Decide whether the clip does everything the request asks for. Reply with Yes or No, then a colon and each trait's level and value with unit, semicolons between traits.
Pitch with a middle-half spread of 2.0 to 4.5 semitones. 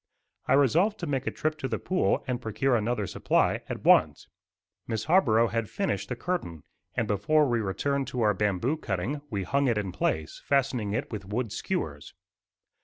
No: average, 5.1 semitones